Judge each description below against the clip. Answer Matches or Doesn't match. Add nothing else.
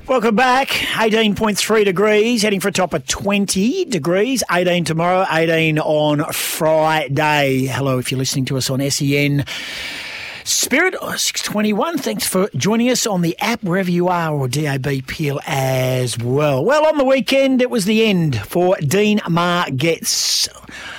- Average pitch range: Doesn't match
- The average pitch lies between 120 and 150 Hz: Doesn't match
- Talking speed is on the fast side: Doesn't match